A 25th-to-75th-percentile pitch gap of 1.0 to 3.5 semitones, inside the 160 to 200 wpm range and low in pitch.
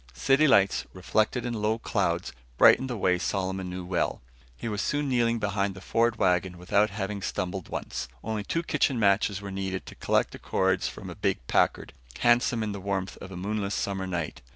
Yes: average, 2.9 semitones; average, 195 wpm; low, 100 Hz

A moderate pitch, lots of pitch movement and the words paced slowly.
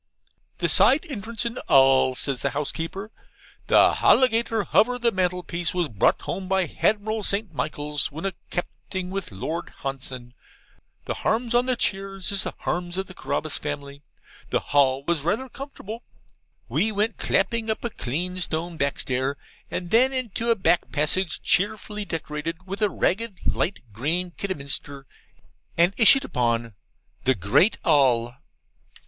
No: medium, 180 Hz; wide, 6.8 semitones; average, 145 wpm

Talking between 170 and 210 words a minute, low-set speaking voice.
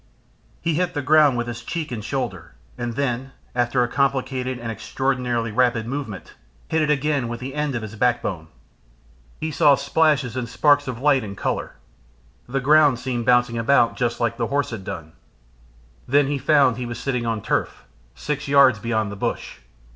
Yes: average, 180 wpm; low, 125 Hz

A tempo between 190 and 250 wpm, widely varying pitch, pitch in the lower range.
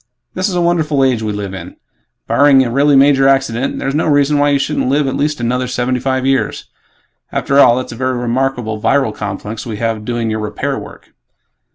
No: fast, 205 wpm; average, 3.3 semitones; low, 130 Hz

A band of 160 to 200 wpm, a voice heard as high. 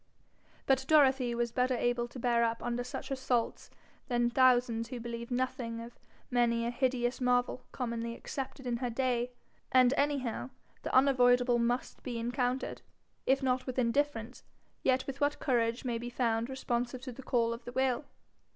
Yes: average, 165 wpm; high, 245 Hz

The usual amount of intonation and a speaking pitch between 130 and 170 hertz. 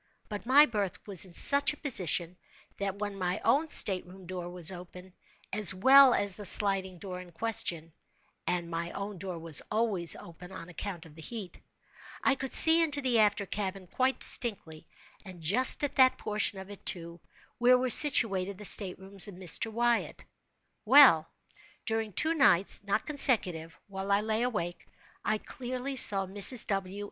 No: average, 4.7 semitones; high, 200 Hz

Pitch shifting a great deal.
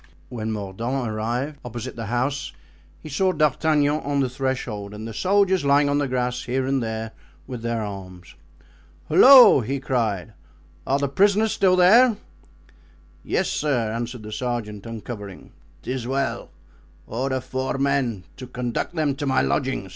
No: average, 4.0 semitones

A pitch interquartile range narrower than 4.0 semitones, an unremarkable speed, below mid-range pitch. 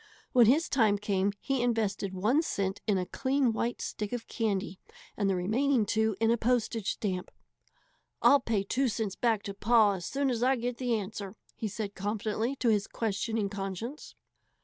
No: average, 3.4 semitones; average, 180 wpm; high, 220 Hz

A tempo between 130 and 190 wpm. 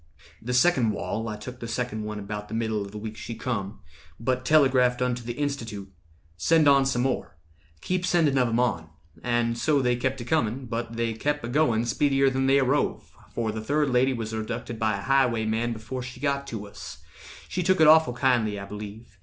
No: fast, 205 wpm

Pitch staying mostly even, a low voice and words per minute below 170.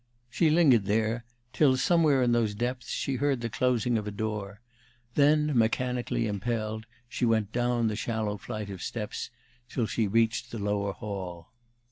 No: average, 3.0 semitones; low, 115 Hz; average, 160 wpm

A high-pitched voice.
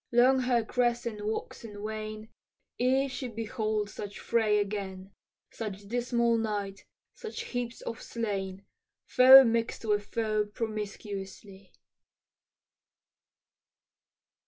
Yes: high, 220 Hz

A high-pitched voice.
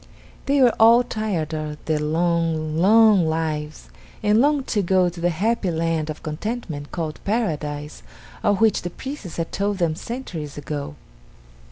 No: medium, 170 Hz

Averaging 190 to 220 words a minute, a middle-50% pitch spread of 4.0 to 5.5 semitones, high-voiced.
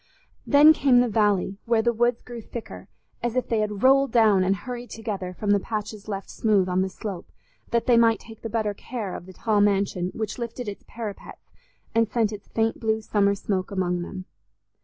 No: average, 200 wpm; average, 2.8 semitones; high, 215 Hz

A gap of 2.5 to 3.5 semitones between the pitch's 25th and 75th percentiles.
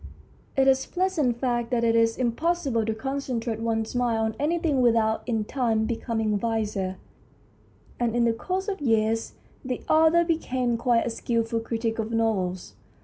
Yes: average, 2.8 semitones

